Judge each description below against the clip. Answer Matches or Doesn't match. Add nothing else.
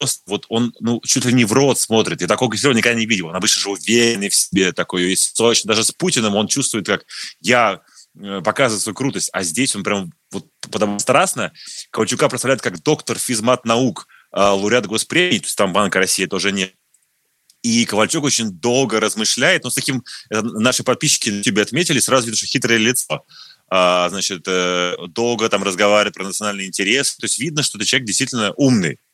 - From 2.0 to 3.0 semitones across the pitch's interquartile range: Doesn't match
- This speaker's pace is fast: Matches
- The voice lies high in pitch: Doesn't match